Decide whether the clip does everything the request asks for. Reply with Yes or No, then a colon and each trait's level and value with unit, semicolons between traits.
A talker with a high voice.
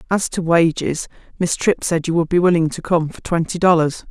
No: medium, 170 Hz